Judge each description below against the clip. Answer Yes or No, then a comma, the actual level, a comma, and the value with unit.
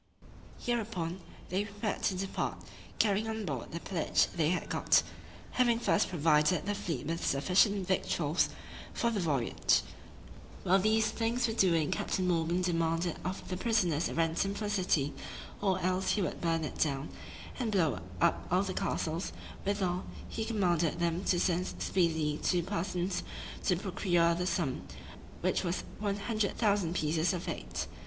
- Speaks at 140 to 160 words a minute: Yes, average, 155 wpm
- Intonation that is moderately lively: Yes, average, 3.4 semitones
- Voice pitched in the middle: Yes, medium, 180 Hz